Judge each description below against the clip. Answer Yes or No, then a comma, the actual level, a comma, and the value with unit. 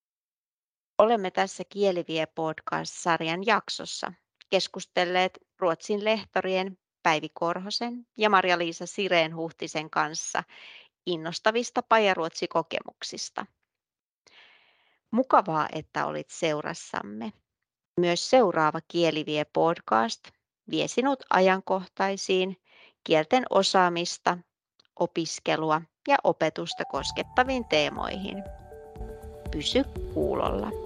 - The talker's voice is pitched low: No, medium, 180 Hz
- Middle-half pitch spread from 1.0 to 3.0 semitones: No, average, 4.3 semitones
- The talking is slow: Yes, slow, 70 wpm